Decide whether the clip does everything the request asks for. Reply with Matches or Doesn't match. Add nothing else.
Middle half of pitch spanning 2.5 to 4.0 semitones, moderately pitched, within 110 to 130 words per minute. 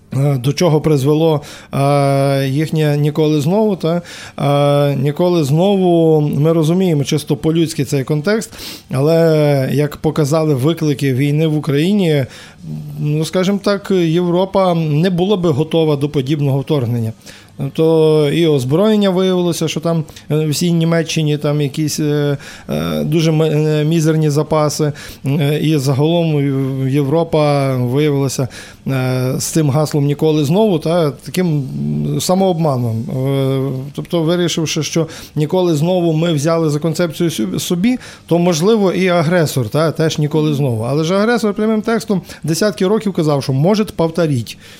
Matches